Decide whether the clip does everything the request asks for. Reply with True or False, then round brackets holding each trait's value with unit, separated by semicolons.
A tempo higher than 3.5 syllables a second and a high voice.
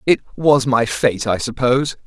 False (4.7 syllables/s; 125 Hz)